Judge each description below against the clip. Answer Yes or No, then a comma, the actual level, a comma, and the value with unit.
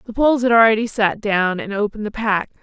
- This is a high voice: Yes, high, 215 Hz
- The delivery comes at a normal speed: No, fast, 230 wpm